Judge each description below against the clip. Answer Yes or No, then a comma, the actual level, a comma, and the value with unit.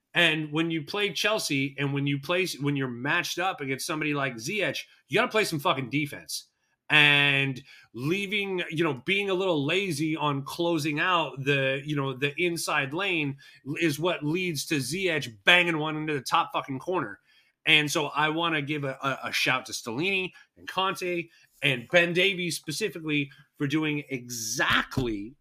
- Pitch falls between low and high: Yes, medium, 155 Hz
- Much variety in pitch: No, average, 3.8 semitones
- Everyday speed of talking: Yes, average, 170 wpm